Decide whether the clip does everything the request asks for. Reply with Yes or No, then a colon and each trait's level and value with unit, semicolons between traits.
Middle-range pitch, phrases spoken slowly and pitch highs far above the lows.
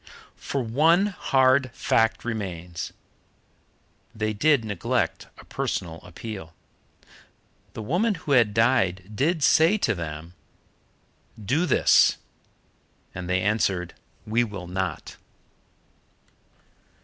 No: low, 110 Hz; slow, 100 wpm; wide, 6.8 semitones